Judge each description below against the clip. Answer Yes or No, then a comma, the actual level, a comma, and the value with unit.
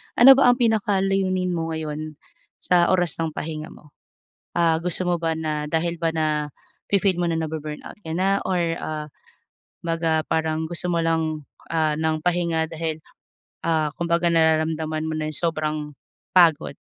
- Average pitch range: No, narrow, 1.9 semitones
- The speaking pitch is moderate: Yes, medium, 160 Hz